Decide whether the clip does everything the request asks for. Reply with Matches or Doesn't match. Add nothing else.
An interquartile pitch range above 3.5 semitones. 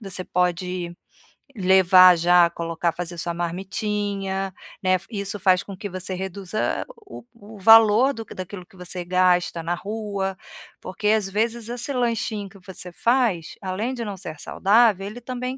Doesn't match